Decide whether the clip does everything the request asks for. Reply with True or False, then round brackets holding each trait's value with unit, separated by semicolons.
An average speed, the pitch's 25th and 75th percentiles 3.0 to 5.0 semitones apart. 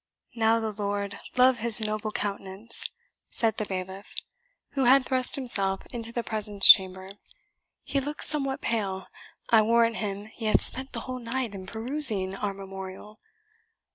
True (150 wpm; 3.4 semitones)